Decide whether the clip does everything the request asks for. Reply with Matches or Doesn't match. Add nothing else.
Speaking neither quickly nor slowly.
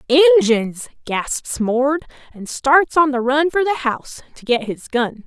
Matches